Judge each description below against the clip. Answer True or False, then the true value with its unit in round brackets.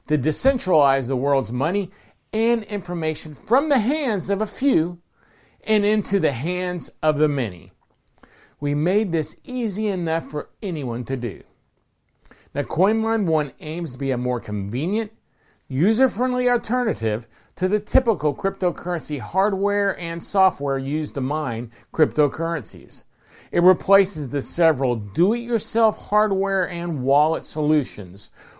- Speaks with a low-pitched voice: False (170 Hz)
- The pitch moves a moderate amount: False (6.4 semitones)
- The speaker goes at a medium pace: False (125 wpm)